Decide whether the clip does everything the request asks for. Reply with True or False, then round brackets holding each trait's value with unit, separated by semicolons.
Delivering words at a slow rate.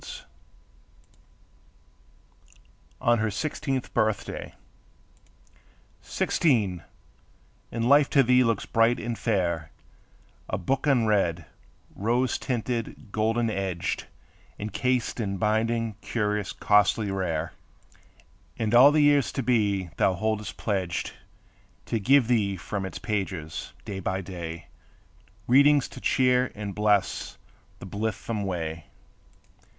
True (110 wpm)